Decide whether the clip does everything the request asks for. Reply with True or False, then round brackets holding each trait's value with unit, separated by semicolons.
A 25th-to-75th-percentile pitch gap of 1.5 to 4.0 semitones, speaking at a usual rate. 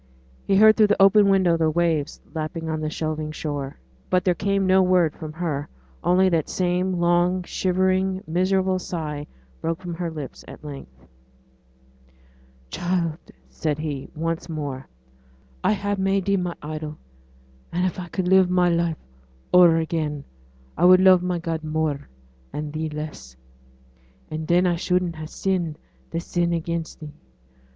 True (2.9 semitones; 155 wpm)